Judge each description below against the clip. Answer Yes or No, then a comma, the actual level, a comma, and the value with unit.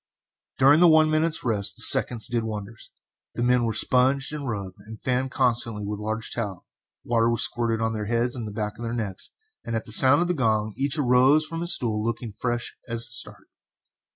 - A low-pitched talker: Yes, low, 120 Hz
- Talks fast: Yes, fast, 225 wpm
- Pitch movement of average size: Yes, average, 3.1 semitones